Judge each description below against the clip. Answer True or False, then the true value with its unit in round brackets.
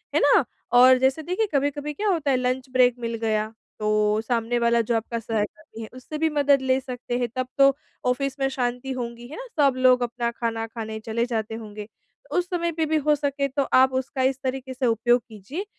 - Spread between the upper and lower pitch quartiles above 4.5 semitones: False (3.1 semitones)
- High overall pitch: True (255 Hz)